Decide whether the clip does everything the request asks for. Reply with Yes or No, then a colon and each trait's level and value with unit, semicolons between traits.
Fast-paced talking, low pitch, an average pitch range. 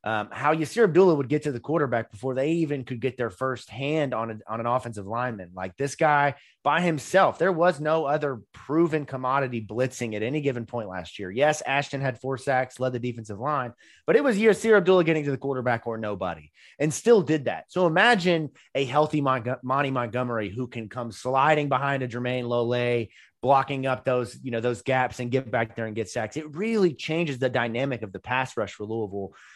Yes: fast, 215 wpm; low, 130 Hz; average, 4.1 semitones